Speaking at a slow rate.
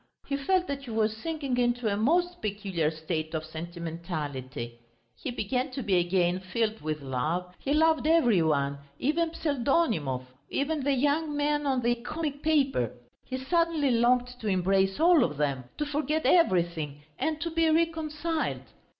No: average, 160 wpm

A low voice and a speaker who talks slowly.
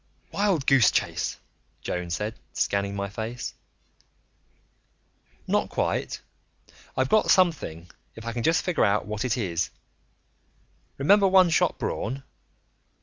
Yes: low, 120 Hz; slow, 120 wpm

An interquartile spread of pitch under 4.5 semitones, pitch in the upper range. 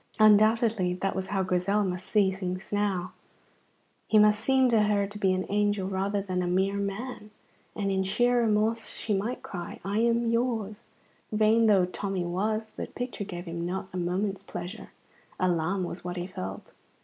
Yes: narrow, 2.6 semitones; high, 200 Hz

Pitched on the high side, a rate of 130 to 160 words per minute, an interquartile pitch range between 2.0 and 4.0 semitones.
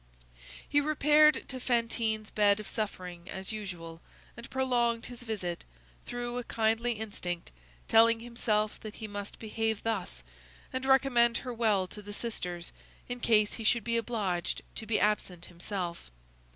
Yes: high, 220 Hz; average, 150 wpm; average, 3.0 semitones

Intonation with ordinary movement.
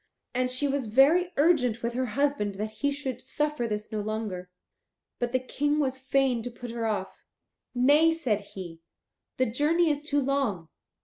Yes: average, 4.7 semitones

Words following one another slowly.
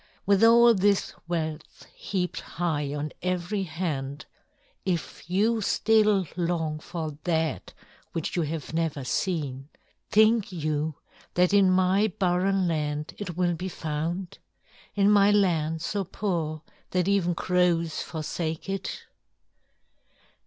Yes: slow, 120 wpm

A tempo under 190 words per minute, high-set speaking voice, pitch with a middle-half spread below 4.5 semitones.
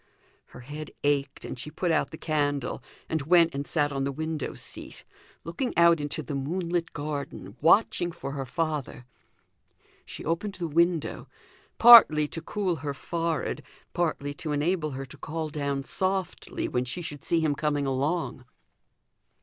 No: average, 160 wpm; medium, 155 Hz; average, 3.1 semitones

